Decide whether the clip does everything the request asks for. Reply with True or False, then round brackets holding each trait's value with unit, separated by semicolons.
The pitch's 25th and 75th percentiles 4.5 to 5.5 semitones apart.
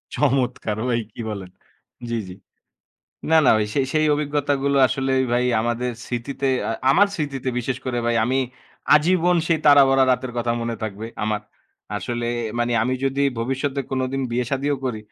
False (3.0 semitones)